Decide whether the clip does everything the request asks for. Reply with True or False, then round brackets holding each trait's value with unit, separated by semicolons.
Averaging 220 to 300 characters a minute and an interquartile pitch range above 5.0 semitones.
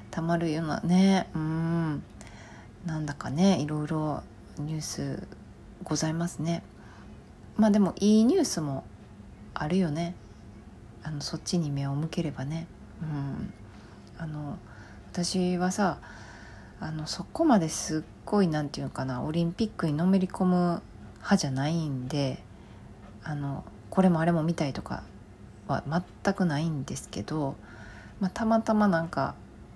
True (265 characters per minute; 5.4 semitones)